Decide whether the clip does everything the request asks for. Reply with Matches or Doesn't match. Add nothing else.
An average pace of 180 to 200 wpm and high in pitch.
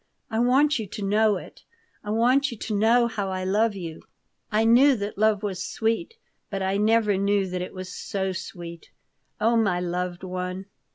Matches